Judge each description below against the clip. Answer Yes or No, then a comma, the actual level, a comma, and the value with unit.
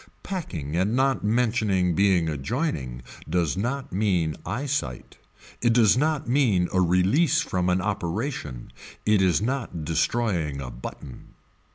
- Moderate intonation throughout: No, wide, 6.8 semitones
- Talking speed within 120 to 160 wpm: Yes, slow, 135 wpm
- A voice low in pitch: Yes, very low, 95 Hz